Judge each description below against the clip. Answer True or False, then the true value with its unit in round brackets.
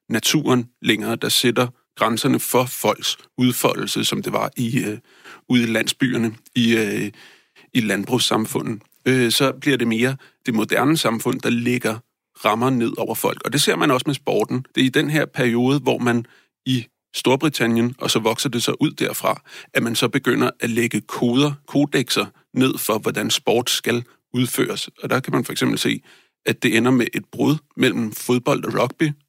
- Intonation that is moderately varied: False (2.3 semitones)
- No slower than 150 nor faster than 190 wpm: True (180 wpm)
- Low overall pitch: True (125 Hz)